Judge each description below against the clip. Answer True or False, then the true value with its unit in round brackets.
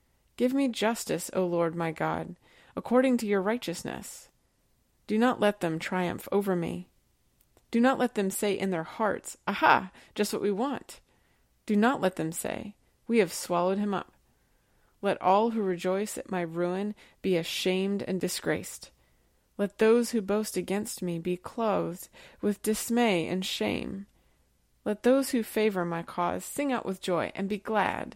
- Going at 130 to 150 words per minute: False (165 wpm)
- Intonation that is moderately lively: True (3.6 semitones)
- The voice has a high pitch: True (200 Hz)